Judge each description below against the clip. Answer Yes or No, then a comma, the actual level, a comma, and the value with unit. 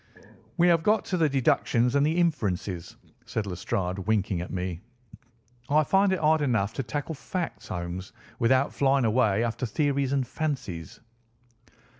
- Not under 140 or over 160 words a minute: Yes, average, 150 wpm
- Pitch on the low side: Yes, low, 125 Hz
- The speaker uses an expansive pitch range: Yes, wide, 7.5 semitones